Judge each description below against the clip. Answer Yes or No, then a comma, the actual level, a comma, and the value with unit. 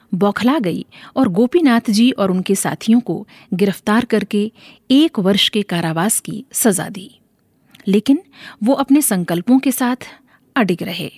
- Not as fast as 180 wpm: Yes, average, 140 wpm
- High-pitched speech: Yes, high, 215 Hz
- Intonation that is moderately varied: Yes, average, 4.2 semitones